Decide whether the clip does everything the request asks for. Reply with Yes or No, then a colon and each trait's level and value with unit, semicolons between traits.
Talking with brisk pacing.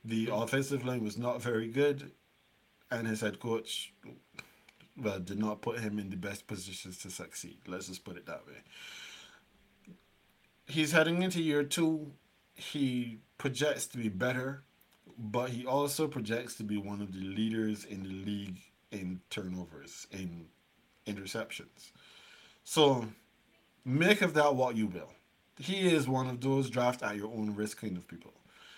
No: average, 155 wpm